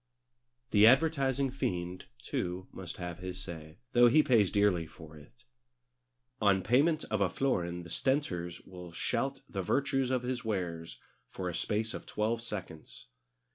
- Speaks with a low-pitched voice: Yes, low, 100 Hz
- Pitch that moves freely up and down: Yes, wide, 6.2 semitones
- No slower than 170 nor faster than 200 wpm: No, average, 150 wpm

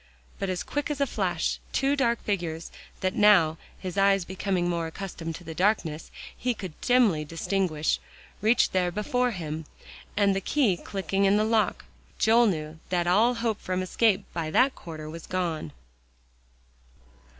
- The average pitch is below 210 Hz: Yes, high, 190 Hz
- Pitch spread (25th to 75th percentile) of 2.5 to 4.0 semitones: No, average, 4.6 semitones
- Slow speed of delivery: No, average, 160 wpm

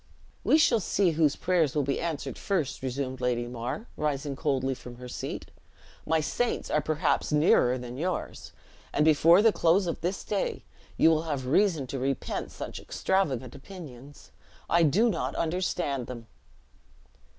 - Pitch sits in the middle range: Yes, medium, 150 Hz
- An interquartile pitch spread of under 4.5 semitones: No, average, 4.9 semitones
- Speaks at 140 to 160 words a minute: Yes, average, 155 wpm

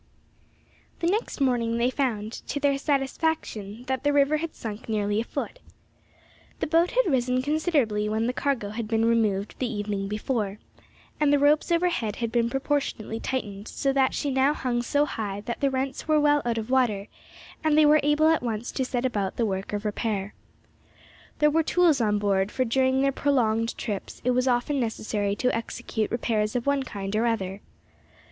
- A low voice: No, high, 245 Hz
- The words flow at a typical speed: Yes, average, 185 wpm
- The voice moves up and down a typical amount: Yes, average, 4.8 semitones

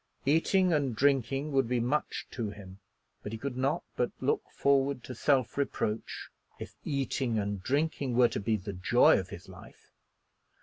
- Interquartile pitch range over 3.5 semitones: Yes, average, 3.9 semitones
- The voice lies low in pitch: Yes, low, 130 Hz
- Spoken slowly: No, average, 170 wpm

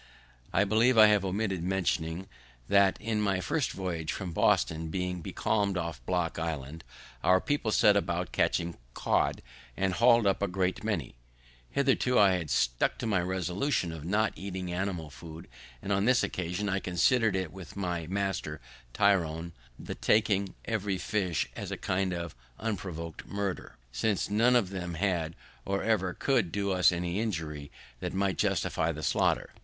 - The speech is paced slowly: No, average, 160 wpm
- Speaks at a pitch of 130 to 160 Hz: No, very low, 95 Hz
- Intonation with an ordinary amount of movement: Yes, average, 3.2 semitones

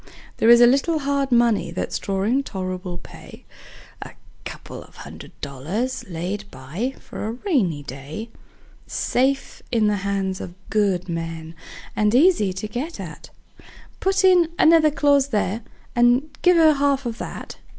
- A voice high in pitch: Yes, high, 230 Hz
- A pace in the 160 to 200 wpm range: No, average, 150 wpm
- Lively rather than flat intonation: Yes, wide, 6.8 semitones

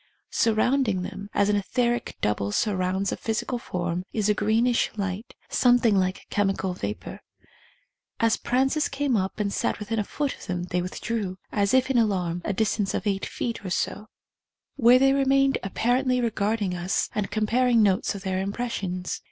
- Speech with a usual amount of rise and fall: Yes, average, 4.1 semitones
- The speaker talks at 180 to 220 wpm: No, average, 170 wpm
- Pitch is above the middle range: Yes, high, 210 Hz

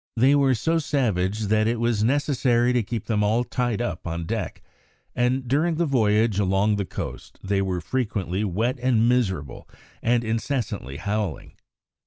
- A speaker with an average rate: Yes, average, 160 wpm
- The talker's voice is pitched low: Yes, low, 115 Hz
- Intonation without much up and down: No, average, 3.9 semitones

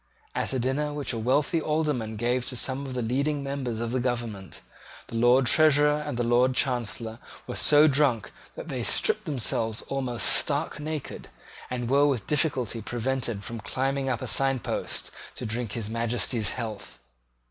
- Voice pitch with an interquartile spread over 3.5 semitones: No, average, 3.2 semitones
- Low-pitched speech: Yes, low, 125 Hz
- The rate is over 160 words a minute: Yes, average, 170 wpm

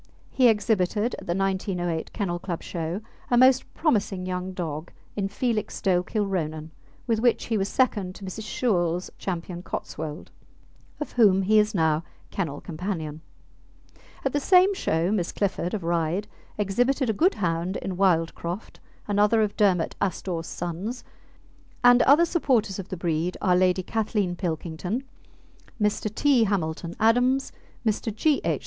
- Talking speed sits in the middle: Yes, average, 145 wpm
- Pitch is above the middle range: Yes, high, 195 Hz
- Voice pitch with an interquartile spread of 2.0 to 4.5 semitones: Yes, average, 4.2 semitones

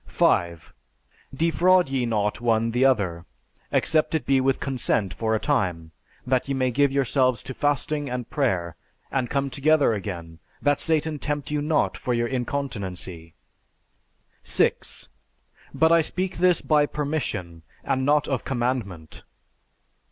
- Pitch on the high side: No, low, 130 Hz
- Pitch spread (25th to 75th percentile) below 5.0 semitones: No, average, 5.3 semitones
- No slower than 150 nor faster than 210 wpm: No, average, 140 wpm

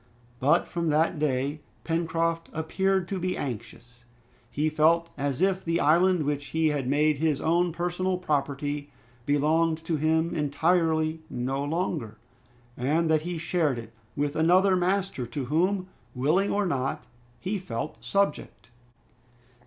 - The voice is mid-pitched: Yes, medium, 160 Hz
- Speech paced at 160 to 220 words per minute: No, slow, 135 wpm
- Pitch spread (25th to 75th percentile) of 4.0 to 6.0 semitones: No, average, 3.4 semitones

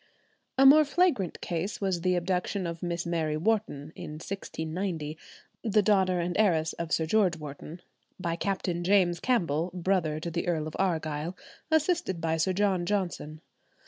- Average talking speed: Yes, average, 155 wpm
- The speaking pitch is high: No, medium, 175 Hz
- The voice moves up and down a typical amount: Yes, average, 3.4 semitones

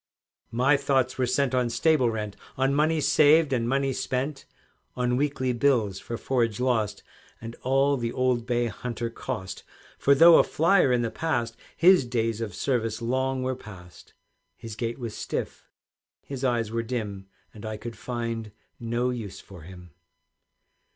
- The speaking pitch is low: Yes, low, 120 Hz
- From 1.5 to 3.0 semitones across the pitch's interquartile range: Yes, average, 2.7 semitones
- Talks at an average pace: Yes, average, 160 wpm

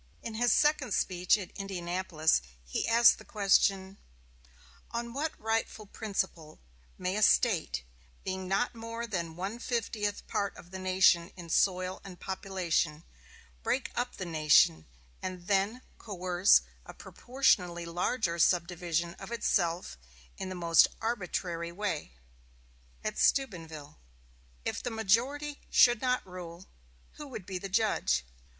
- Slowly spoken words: Yes, slow, 130 wpm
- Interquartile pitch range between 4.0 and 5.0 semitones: Yes, average, 4.5 semitones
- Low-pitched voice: No, high, 190 Hz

